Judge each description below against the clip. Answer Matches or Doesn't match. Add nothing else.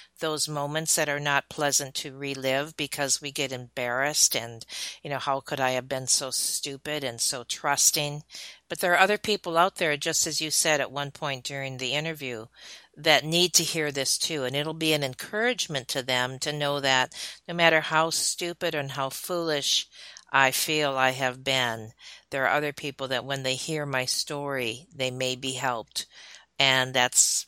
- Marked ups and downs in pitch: Doesn't match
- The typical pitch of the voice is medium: Matches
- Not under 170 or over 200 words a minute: Matches